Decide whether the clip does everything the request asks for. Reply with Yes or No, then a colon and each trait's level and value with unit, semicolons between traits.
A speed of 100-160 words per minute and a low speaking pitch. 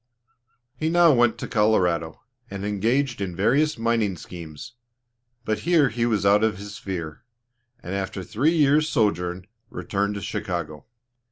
Yes: average, 150 wpm; low, 105 Hz